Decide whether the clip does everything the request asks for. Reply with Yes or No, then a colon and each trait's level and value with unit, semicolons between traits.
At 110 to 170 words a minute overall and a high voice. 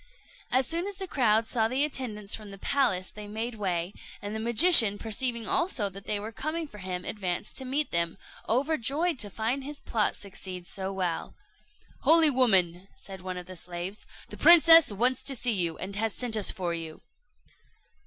No: average, 185 wpm; high, 220 Hz